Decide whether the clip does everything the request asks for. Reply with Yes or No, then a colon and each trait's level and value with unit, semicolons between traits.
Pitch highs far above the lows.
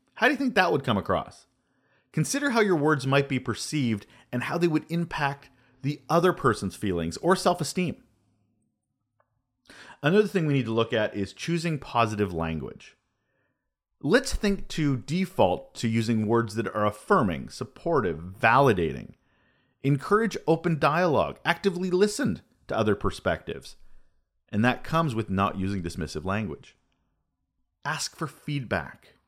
Yes: wide, 8.6 semitones